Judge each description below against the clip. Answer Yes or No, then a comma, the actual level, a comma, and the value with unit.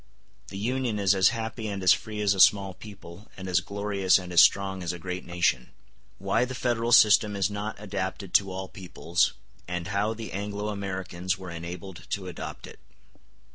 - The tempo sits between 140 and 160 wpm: No, average, 185 wpm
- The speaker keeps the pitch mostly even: Yes, narrow, 2.2 semitones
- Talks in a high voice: No, very low, 95 Hz